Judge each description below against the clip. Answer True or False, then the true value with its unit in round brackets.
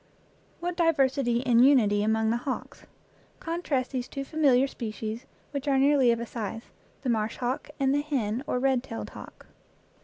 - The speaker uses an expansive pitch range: False (3.2 semitones)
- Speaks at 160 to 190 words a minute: True (175 wpm)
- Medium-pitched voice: False (255 Hz)